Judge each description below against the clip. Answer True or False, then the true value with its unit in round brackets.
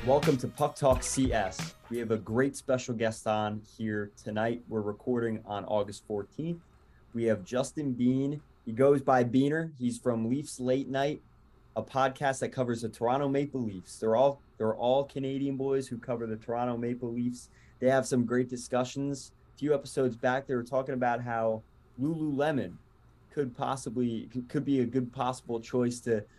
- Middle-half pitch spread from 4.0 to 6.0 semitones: False (2.8 semitones)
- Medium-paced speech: True (175 wpm)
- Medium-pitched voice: False (125 Hz)